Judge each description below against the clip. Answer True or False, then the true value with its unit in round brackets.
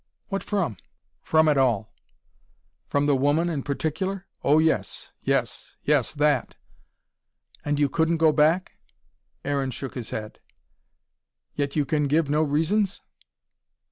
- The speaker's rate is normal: False (130 wpm)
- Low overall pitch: False (150 Hz)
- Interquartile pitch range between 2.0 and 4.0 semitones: True (2.4 semitones)